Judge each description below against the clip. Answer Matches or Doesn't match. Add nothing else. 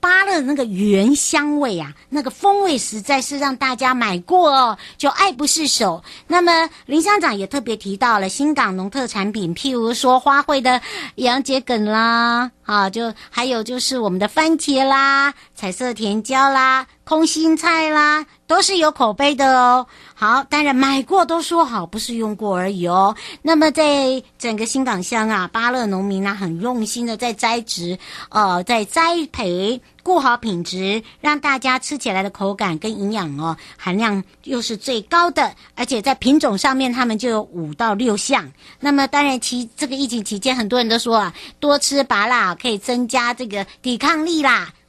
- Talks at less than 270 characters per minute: Matches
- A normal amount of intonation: Matches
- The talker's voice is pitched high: Matches